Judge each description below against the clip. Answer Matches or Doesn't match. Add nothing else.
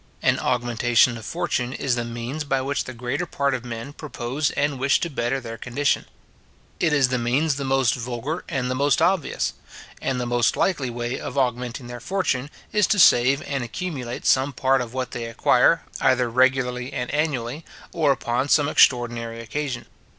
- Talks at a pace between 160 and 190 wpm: Matches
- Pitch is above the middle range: Doesn't match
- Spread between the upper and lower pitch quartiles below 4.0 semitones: Matches